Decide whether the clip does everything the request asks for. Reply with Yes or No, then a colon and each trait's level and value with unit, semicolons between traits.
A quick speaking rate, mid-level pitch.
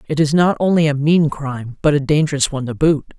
Yes: fast, 245 wpm; medium, 150 Hz